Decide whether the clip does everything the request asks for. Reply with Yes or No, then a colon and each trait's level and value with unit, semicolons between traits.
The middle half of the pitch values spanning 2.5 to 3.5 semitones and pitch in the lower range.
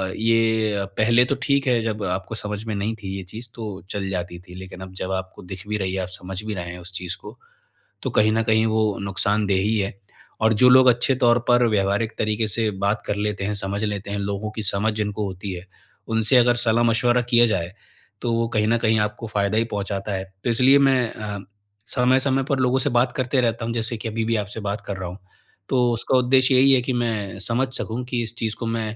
Yes: average, 3.0 semitones; low, 110 Hz